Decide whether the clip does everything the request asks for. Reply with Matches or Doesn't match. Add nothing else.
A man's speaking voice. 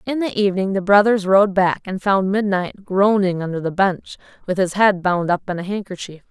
Doesn't match